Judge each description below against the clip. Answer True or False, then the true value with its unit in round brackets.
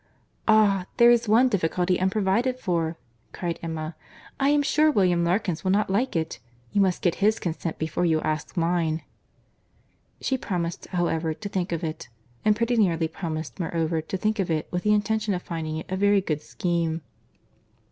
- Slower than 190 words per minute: True (175 wpm)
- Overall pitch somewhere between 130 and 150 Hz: False (180 Hz)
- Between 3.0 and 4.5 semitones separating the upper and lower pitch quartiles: True (4.2 semitones)